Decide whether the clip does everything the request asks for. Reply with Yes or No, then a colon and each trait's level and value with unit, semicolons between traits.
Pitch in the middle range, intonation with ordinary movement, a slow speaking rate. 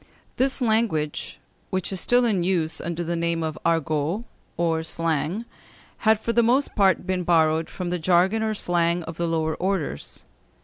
No: medium, 175 Hz; average, 4.0 semitones; average, 170 wpm